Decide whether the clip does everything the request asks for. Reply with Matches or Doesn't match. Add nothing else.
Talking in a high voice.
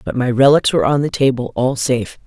Doesn't match